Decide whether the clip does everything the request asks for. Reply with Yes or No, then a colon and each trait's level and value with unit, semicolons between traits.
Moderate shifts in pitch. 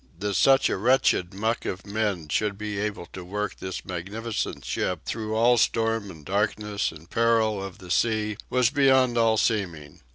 Yes: average, 3.1 semitones